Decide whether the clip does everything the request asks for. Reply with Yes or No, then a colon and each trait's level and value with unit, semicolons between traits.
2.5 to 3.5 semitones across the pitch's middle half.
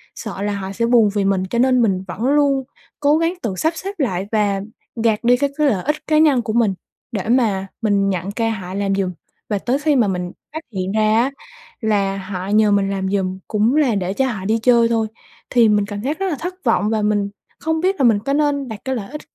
No: average, 5.1 semitones